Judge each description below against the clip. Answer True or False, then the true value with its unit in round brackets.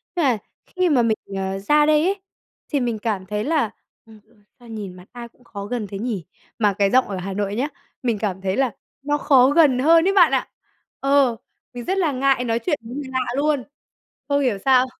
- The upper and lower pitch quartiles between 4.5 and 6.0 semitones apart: True (5.4 semitones)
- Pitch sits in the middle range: False (245 Hz)